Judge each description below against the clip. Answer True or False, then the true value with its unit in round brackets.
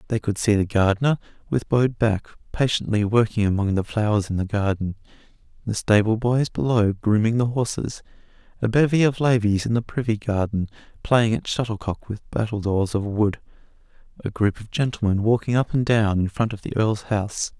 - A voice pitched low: True (110 Hz)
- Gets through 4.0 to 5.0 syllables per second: False (5.4 syllables/s)